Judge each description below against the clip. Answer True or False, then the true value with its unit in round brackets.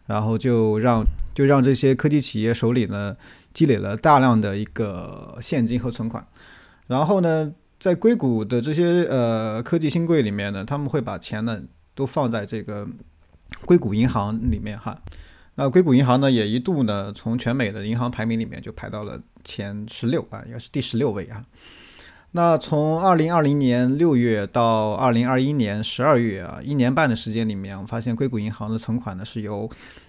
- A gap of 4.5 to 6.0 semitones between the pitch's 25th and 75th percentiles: False (4.0 semitones)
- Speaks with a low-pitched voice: True (115 Hz)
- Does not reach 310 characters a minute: True (275 characters per minute)